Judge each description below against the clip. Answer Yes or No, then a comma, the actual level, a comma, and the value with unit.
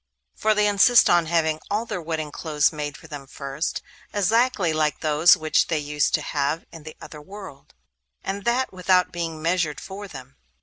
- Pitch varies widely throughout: No, average, 4.3 semitones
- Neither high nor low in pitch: Yes, medium, 165 Hz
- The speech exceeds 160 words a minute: Yes, average, 180 wpm